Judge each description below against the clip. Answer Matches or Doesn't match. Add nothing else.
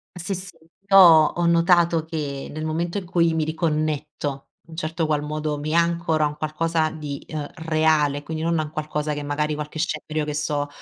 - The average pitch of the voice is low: Doesn't match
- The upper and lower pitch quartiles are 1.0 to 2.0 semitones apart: Matches